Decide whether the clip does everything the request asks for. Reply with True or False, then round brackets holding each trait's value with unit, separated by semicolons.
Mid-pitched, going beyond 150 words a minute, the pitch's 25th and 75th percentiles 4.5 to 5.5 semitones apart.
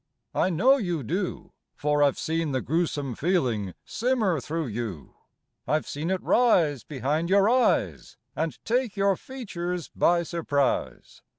False (165 Hz; 135 wpm; 5.2 semitones)